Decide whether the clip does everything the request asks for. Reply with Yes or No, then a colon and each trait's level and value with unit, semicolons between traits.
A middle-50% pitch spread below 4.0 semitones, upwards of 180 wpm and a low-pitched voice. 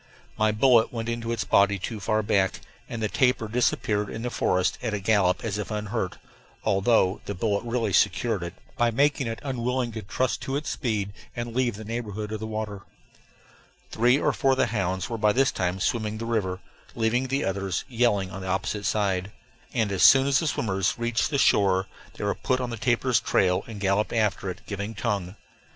Yes: average, 3.2 semitones; fast, 205 wpm; low, 110 Hz